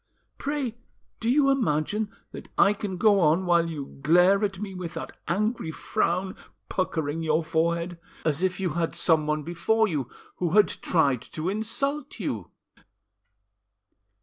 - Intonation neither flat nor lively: Yes, average, 4.6 semitones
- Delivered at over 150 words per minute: No, average, 145 wpm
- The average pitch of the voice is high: No, medium, 180 Hz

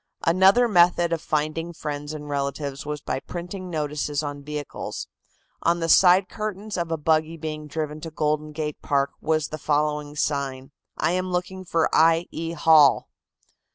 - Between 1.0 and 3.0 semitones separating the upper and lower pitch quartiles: Yes, narrow, 2.6 semitones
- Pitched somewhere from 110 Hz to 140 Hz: No, medium, 155 Hz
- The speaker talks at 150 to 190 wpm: Yes, average, 160 wpm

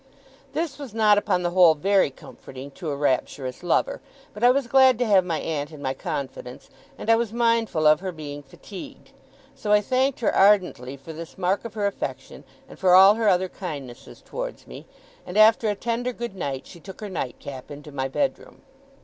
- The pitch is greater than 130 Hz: Yes, high, 190 Hz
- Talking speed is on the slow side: No, average, 200 wpm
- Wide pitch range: Yes, wide, 7.6 semitones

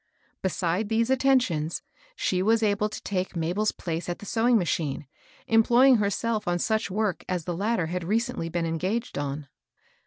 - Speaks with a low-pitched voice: No, high, 200 Hz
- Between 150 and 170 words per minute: Yes, average, 160 wpm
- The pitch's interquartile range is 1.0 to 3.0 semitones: No, average, 4.7 semitones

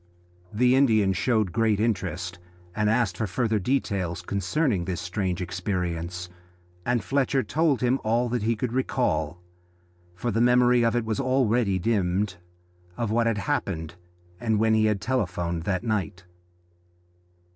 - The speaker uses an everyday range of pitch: Yes, average, 4.6 semitones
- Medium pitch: No, low, 110 Hz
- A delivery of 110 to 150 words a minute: Yes, average, 140 wpm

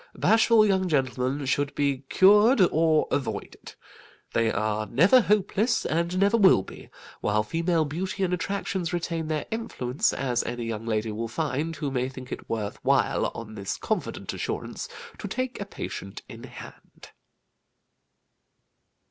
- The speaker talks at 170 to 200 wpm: No, average, 145 wpm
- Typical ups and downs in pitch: No, wide, 7.6 semitones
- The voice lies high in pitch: No, medium, 155 Hz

